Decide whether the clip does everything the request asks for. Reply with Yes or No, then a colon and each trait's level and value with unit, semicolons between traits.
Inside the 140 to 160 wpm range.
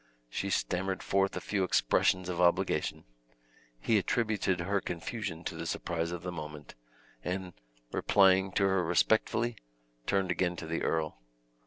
Yes: average, 145 wpm